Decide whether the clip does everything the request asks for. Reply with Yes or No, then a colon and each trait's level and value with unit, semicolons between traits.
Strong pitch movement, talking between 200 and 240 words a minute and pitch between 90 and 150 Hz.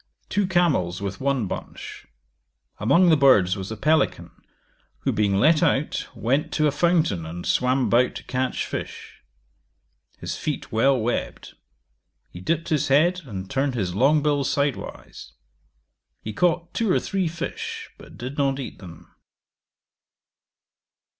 No: wide, 6.5 semitones; average, 140 wpm; low, 135 Hz